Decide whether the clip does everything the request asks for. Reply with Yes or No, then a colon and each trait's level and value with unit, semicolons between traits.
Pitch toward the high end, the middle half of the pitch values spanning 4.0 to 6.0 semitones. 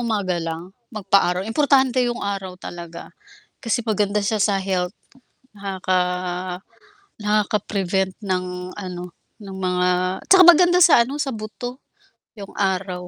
No: high, 195 Hz; average, 3.5 semitones